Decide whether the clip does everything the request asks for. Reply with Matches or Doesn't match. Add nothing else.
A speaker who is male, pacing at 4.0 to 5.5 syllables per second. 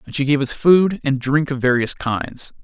Matches